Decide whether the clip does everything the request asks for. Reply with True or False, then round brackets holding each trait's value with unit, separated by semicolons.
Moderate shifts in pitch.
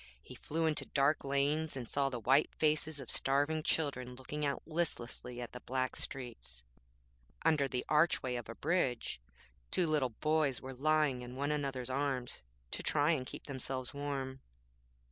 True (3.0 semitones)